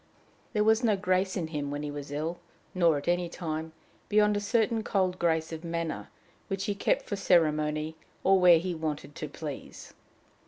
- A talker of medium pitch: Yes, medium, 170 Hz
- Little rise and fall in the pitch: No, average, 3.9 semitones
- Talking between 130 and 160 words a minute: No, average, 185 wpm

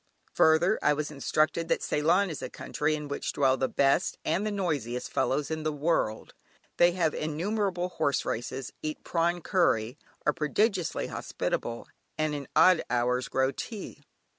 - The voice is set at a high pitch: No, medium, 155 Hz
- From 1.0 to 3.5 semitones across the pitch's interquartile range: No, average, 4.0 semitones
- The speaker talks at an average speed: Yes, average, 160 wpm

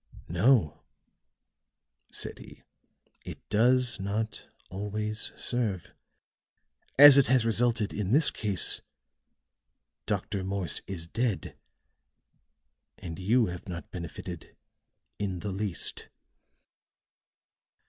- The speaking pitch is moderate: No, low, 105 Hz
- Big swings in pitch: No, average, 4.2 semitones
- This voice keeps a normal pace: No, slow, 90 wpm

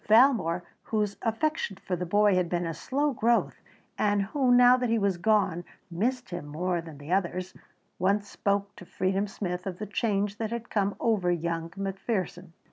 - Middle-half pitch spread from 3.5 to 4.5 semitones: Yes, average, 3.8 semitones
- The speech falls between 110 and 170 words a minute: No, average, 180 wpm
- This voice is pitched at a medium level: No, high, 200 Hz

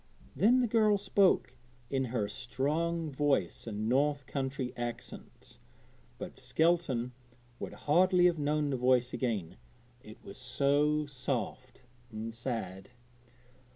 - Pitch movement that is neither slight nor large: Yes, average, 4.0 semitones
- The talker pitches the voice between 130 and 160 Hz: Yes, low, 135 Hz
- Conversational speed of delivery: No, slow, 120 wpm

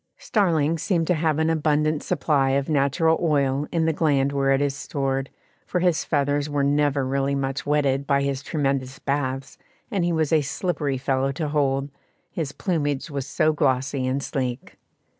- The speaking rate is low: No, average, 175 wpm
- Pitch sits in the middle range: Yes, medium, 145 Hz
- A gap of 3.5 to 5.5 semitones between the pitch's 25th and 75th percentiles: No, narrow, 2.4 semitones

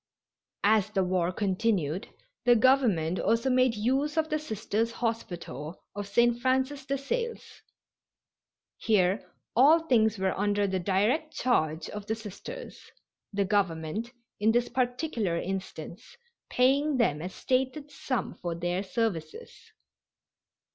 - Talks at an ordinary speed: No, slow, 125 wpm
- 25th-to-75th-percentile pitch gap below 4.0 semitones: No, wide, 5.4 semitones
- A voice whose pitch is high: Yes, high, 220 Hz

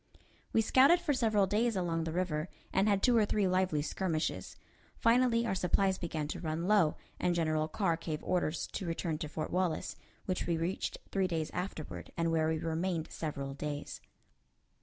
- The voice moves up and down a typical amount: Yes, average, 3.7 semitones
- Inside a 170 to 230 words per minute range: Yes, average, 180 wpm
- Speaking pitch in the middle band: Yes, medium, 175 Hz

